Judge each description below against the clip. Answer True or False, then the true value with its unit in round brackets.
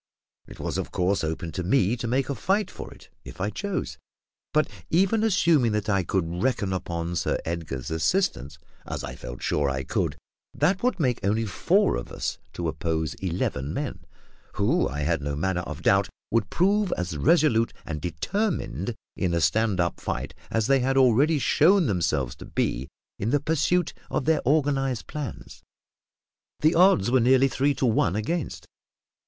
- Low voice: True (110 Hz)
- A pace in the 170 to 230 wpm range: True (175 wpm)